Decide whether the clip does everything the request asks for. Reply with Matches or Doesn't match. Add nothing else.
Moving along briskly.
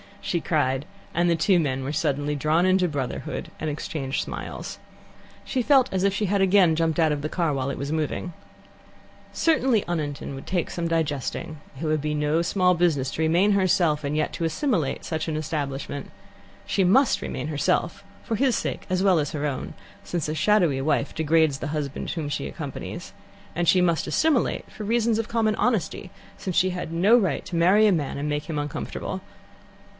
Doesn't match